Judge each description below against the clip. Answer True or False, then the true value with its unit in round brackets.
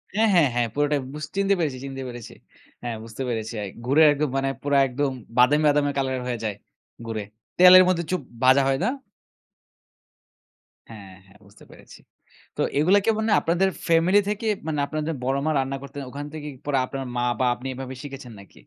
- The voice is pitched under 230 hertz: True (140 Hz)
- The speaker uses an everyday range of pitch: True (4.0 semitones)